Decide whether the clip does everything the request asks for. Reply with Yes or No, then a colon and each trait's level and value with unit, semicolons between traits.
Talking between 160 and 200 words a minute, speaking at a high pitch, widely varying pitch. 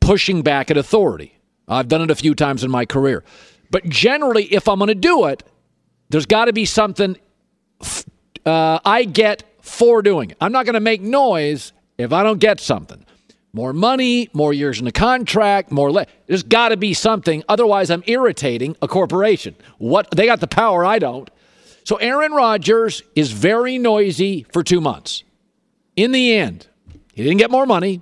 Yes: average, 185 wpm; high, 200 Hz; wide, 6.2 semitones